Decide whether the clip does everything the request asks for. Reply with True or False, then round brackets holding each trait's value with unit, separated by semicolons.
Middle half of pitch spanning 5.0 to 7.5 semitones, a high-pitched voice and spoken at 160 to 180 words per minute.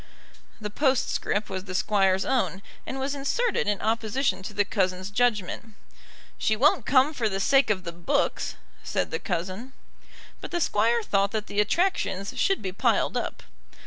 True (5.4 semitones; 210 Hz; 165 wpm)